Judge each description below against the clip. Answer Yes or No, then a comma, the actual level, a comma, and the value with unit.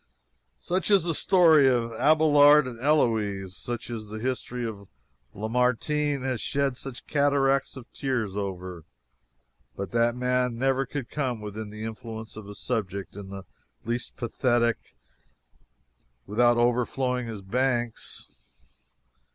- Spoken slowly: Yes, slow, 125 wpm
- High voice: No, low, 120 Hz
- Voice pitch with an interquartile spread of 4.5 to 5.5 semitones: No, average, 3.6 semitones